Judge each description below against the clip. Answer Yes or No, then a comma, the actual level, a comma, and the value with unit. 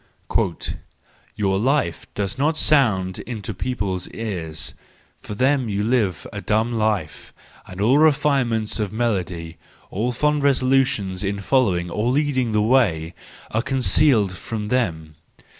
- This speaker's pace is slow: Yes, slow, 130 wpm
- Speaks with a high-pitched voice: No, low, 110 Hz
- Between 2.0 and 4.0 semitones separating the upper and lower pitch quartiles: No, average, 5.2 semitones